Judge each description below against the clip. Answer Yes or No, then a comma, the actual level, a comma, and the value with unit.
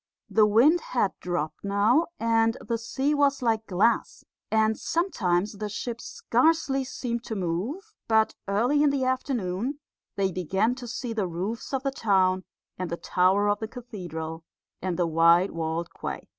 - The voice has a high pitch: Yes, high, 220 Hz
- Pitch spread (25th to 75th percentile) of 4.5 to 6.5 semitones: Yes, average, 5.3 semitones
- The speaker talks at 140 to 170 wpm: Yes, average, 160 wpm